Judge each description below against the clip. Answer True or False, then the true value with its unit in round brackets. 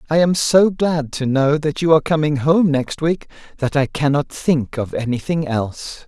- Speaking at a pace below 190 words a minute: False (205 wpm)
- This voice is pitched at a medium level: True (150 Hz)